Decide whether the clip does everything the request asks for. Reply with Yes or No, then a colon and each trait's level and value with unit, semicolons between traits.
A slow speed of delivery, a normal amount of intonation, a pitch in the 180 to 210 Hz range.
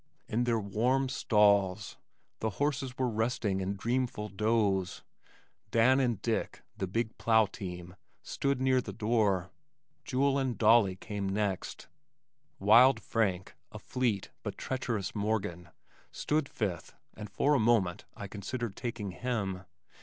No: slow, 130 wpm; average, 4.0 semitones; low, 110 Hz